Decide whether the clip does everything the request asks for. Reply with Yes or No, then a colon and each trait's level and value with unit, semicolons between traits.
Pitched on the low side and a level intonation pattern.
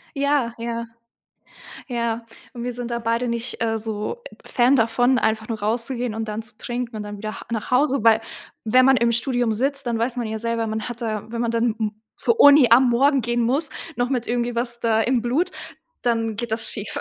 No: high, 235 Hz; narrow, 1.7 semitones